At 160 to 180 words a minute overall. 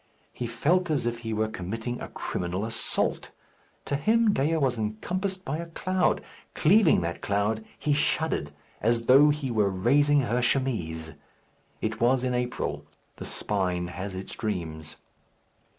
No: average, 150 wpm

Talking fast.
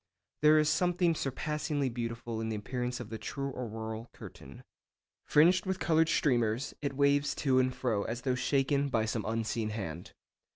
No: average, 165 wpm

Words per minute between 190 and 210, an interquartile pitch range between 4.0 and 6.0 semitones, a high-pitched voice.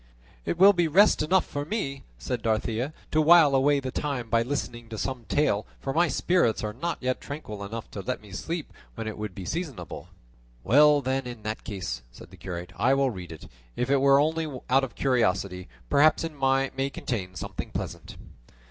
No: average, 195 wpm; wide, 5.4 semitones; low, 130 Hz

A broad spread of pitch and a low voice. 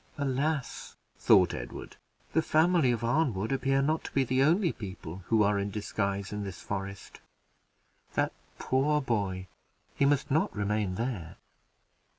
Yes: wide, 5.9 semitones; low, 115 Hz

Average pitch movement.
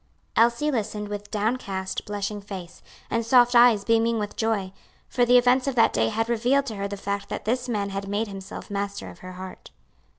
Yes: average, 3.0 semitones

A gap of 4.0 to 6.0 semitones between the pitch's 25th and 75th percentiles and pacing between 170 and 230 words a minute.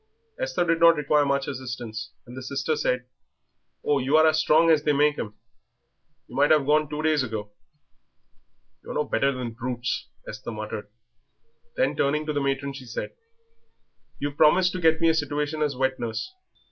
No: average, 3.2 semitones; average, 180 wpm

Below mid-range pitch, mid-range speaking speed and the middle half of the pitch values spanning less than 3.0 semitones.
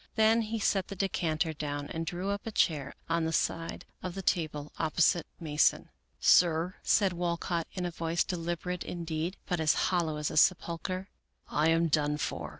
No: medium, 170 Hz; average, 185 wpm; narrow, 2.5 semitones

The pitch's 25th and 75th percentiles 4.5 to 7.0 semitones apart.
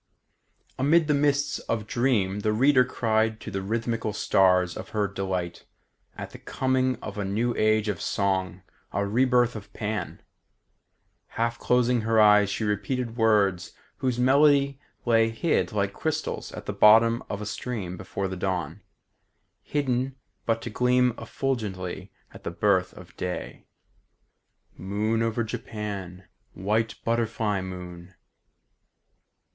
No: average, 4.1 semitones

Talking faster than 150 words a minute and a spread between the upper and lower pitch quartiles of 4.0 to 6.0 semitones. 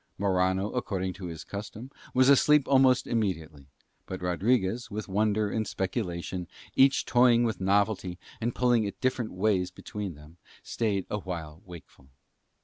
No: average, 140 wpm; average, 4.4 semitones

